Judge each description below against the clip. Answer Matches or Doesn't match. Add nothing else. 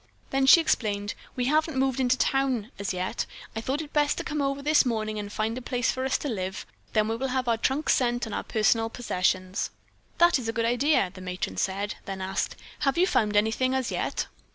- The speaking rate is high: Matches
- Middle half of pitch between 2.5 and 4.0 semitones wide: Doesn't match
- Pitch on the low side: Doesn't match